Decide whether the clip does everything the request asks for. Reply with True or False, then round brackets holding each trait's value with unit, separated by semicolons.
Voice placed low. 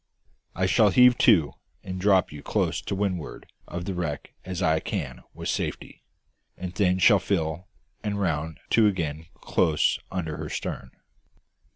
True (90 Hz)